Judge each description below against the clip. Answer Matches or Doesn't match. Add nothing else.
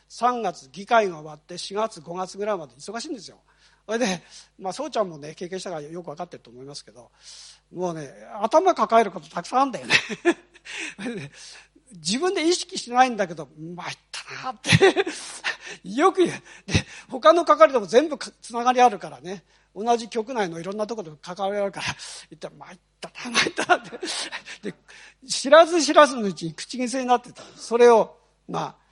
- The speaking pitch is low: Doesn't match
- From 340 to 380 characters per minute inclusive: Matches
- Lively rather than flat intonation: Matches